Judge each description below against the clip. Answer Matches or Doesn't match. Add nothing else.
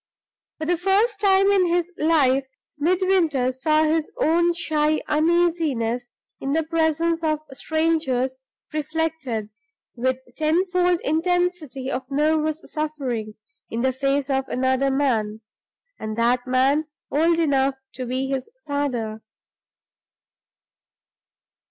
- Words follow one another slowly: Matches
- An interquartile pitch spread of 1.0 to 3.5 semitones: Doesn't match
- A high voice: Matches